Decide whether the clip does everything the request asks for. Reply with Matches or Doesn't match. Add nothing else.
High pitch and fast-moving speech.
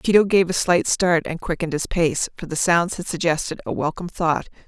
Doesn't match